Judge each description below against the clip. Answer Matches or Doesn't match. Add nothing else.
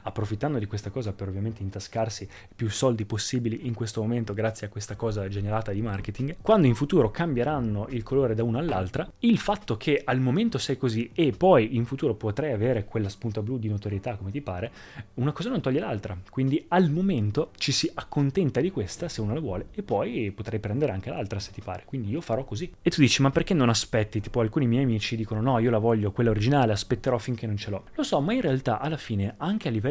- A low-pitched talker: Matches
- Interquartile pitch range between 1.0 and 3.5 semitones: Doesn't match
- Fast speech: Matches